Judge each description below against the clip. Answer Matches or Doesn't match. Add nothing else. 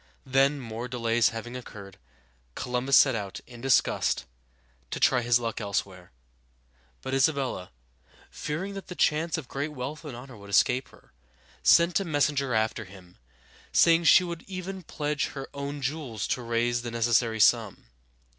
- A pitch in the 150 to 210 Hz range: Doesn't match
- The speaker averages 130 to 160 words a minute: Matches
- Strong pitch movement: Doesn't match